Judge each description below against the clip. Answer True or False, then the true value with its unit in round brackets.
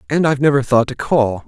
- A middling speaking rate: False (245 wpm)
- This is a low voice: True (130 Hz)